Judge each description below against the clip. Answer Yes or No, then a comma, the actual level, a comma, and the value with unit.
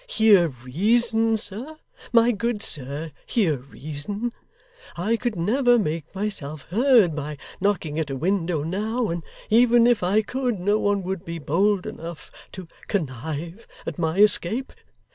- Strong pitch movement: Yes, wide, 5.8 semitones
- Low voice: No, high, 195 Hz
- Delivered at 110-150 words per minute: Yes, average, 145 wpm